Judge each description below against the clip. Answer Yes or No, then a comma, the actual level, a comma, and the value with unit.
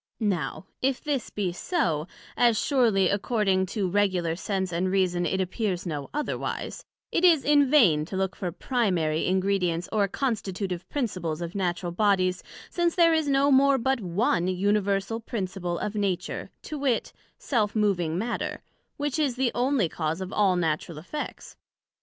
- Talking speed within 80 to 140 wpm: No, average, 155 wpm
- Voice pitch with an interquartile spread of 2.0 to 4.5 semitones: No, wide, 5.6 semitones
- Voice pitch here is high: Yes, high, 195 Hz